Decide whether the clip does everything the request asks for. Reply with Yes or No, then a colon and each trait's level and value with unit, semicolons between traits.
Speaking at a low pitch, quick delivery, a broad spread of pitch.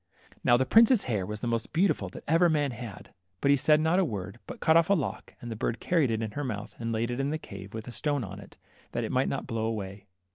Yes: low, 120 Hz; fast, 280 wpm; wide, 6.2 semitones